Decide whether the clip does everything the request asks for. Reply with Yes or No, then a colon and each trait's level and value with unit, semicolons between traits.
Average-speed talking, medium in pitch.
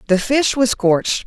No: average, 190 wpm; high, 225 Hz